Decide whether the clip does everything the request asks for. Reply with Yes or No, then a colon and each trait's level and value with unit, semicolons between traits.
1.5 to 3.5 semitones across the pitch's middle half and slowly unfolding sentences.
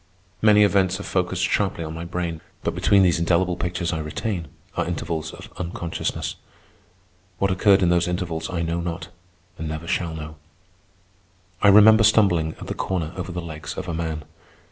No: narrow, 2.4 semitones; average, 175 wpm